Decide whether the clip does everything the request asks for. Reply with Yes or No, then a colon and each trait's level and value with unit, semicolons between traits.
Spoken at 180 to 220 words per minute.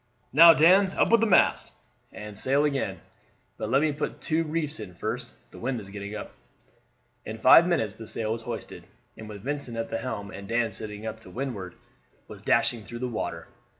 Yes: average, 200 wpm